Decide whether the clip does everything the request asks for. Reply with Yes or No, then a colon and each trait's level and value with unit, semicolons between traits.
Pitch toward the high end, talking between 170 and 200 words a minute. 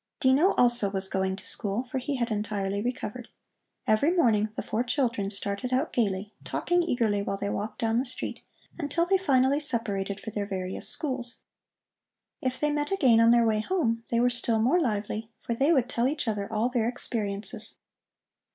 Yes: high, 235 Hz; average, 185 wpm